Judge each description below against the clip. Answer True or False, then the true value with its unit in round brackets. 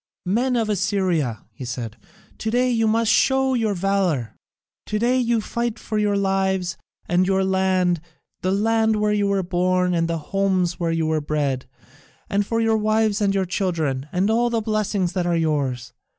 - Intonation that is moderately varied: True (4.0 semitones)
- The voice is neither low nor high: False (195 Hz)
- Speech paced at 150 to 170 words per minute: False (180 wpm)